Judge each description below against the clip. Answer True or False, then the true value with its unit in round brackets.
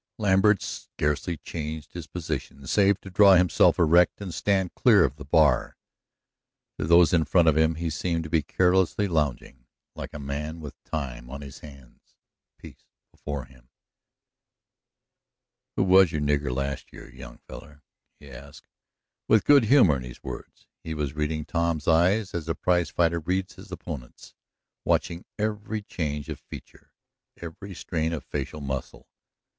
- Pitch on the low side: True (80 Hz)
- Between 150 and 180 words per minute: True (155 wpm)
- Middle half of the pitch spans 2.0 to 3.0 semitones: False (4.0 semitones)